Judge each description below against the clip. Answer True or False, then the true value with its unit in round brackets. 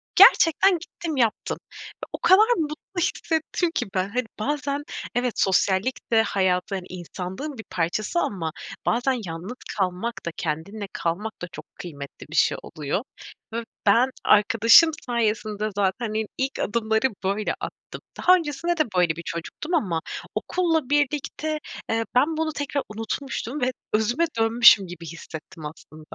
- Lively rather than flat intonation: True (7.5 semitones)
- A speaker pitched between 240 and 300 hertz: False (225 Hz)